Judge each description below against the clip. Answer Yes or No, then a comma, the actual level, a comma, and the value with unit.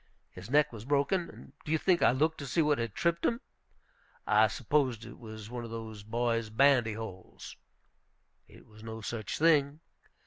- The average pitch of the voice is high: No, low, 120 Hz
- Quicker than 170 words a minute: Yes, average, 180 wpm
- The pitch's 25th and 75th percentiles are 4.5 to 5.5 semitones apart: Yes, average, 5.0 semitones